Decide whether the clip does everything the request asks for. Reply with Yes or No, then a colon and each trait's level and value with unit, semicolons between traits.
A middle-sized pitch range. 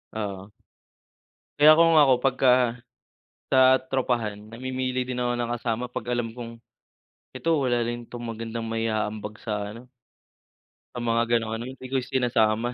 No: narrow, 2.3 semitones